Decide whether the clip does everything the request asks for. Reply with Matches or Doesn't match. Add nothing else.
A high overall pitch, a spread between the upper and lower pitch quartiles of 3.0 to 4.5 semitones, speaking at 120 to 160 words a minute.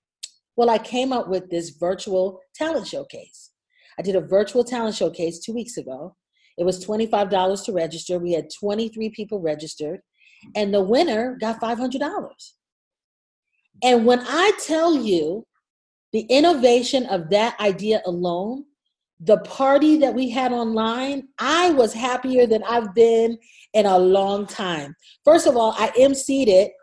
Doesn't match